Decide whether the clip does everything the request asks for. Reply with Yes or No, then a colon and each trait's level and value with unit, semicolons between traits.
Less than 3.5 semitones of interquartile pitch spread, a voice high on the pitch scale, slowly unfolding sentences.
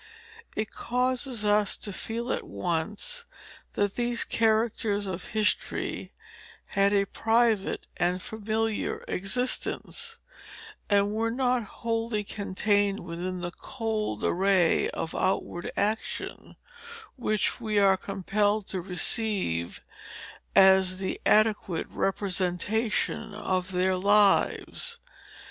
Yes: average, 2.9 semitones; high, 205 Hz; slow, 100 wpm